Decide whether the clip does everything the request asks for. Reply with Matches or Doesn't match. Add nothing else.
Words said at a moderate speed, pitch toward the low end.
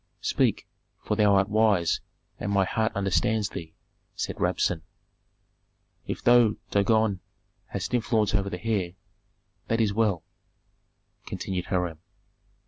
Doesn't match